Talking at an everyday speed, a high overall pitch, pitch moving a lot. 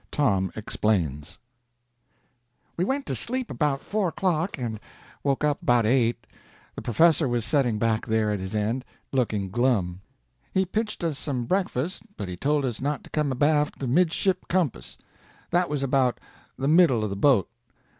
No: average, 165 wpm; low, 135 Hz; wide, 6.4 semitones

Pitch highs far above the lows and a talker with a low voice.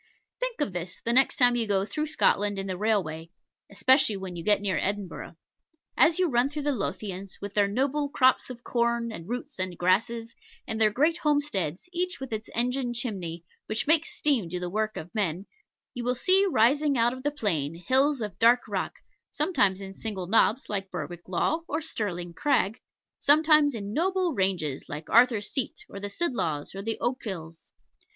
No: wide, 6.0 semitones; high, 225 Hz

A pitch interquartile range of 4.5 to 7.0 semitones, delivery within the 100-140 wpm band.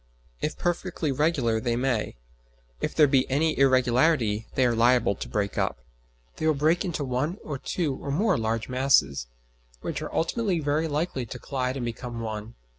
No: average, 4.9 semitones; average, 175 wpm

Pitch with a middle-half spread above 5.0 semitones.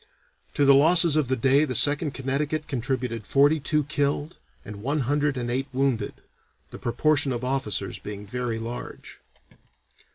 No: average, 3.2 semitones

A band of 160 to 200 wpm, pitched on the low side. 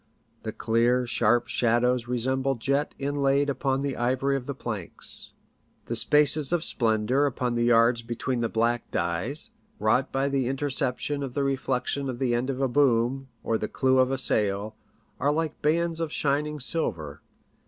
Yes: average, 165 wpm; low, 130 Hz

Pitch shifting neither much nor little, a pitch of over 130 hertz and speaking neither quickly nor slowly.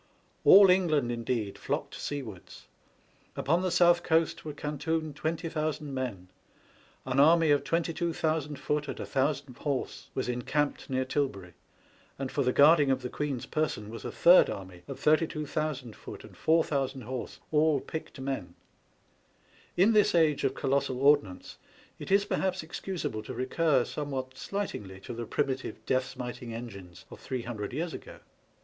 Yes: average, 4.1 semitones; medium, 140 Hz; average, 150 wpm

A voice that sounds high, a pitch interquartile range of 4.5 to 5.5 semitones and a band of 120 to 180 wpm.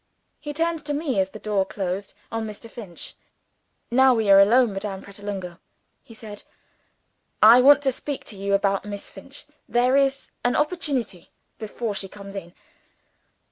Yes: high, 215 Hz; average, 5.0 semitones; average, 160 wpm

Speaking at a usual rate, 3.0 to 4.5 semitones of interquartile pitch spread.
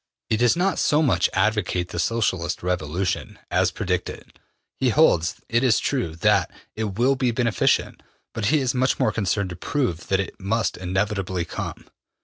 No: average, 170 wpm; average, 5.1 semitones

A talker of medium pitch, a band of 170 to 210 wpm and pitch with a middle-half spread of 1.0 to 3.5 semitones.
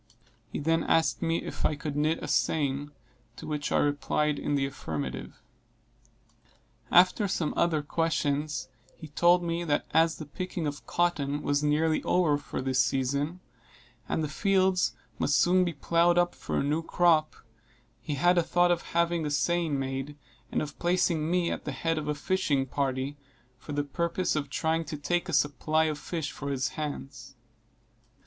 Yes: medium, 155 Hz; average, 175 wpm; average, 3.0 semitones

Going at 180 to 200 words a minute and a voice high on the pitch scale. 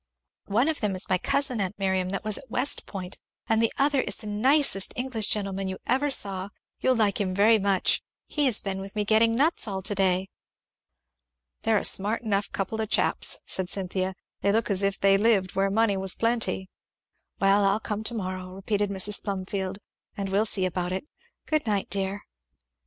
Yes: average, 195 wpm; high, 200 Hz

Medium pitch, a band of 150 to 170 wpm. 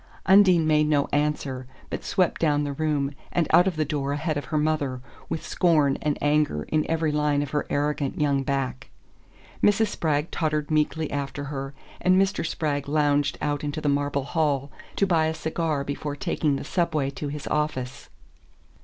No: medium, 150 Hz; average, 180 wpm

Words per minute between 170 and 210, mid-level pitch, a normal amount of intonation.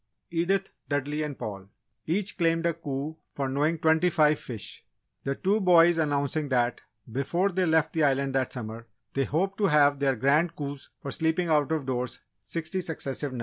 Yes: average, 180 wpm; medium, 150 Hz; average, 3.5 semitones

